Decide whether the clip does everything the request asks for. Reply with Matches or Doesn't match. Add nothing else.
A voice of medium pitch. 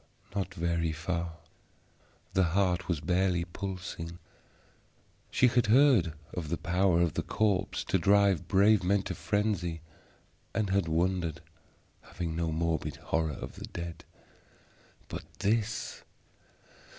Doesn't match